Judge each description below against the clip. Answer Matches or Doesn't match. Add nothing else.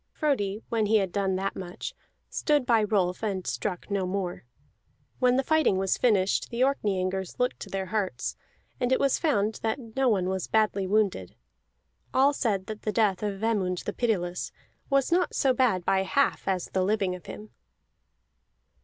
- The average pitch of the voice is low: Doesn't match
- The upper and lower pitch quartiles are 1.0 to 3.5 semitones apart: Doesn't match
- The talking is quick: Doesn't match